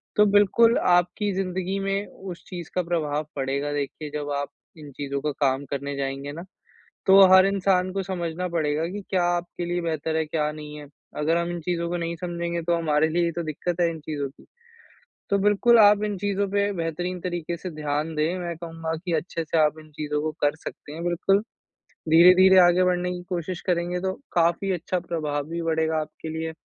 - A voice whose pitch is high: No, medium, 170 Hz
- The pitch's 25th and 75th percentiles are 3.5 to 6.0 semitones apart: No, average, 2.9 semitones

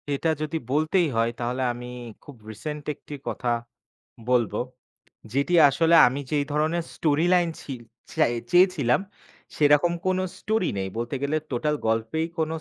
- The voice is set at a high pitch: No, medium, 150 Hz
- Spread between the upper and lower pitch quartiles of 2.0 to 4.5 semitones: No, average, 5.0 semitones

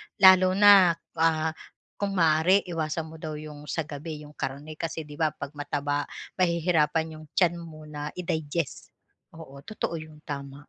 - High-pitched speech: No, medium, 155 Hz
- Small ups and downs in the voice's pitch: Yes, narrow, 2.2 semitones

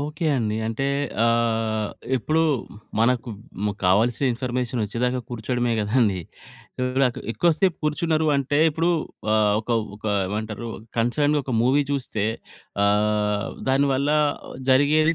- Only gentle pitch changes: No, average, 4.5 semitones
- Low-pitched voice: Yes, low, 120 Hz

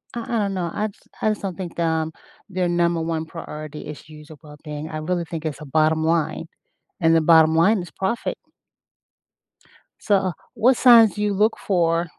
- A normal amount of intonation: Yes, average, 3.6 semitones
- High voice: No, medium, 170 Hz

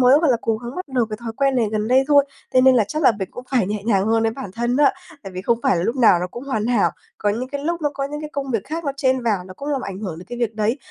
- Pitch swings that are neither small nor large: Yes, average, 4.3 semitones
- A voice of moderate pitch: No, high, 240 Hz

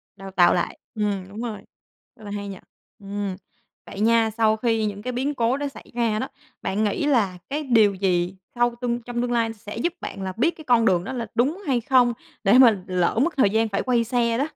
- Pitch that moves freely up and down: No, average, 3.3 semitones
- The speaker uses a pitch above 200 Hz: Yes, high, 225 Hz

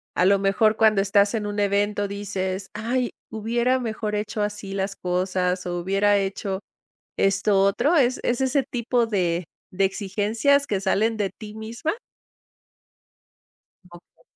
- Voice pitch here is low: No, high, 205 Hz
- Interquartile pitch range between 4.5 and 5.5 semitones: No, narrow, 2.4 semitones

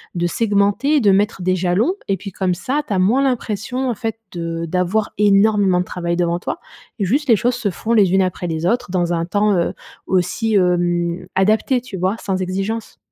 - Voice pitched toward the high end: Yes, high, 195 Hz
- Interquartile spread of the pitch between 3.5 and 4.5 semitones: Yes, average, 3.8 semitones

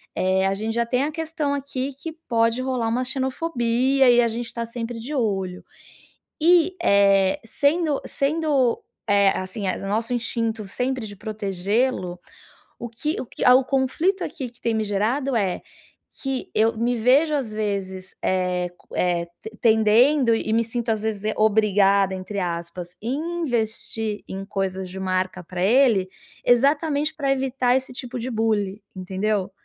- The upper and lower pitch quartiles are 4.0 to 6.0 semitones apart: Yes, average, 4.8 semitones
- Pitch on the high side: Yes, high, 230 Hz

